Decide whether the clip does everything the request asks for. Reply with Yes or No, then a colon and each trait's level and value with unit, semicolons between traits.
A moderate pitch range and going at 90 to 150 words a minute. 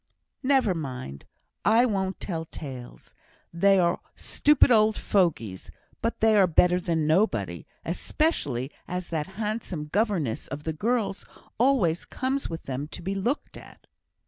No: wide, 5.9 semitones; average, 140 wpm